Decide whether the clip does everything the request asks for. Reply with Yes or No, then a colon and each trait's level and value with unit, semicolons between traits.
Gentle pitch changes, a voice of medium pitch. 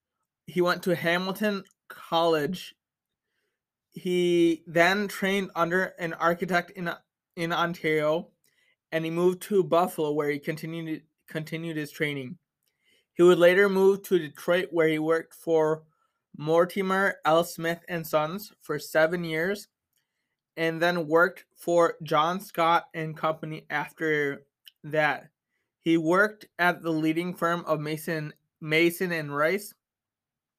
Yes: narrow, 2.2 semitones; medium, 170 Hz